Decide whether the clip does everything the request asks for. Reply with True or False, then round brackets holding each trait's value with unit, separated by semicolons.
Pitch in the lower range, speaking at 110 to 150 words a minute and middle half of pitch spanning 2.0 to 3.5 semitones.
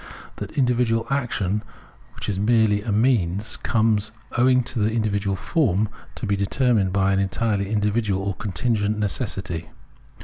True (105 Hz; 140 wpm; 2.8 semitones)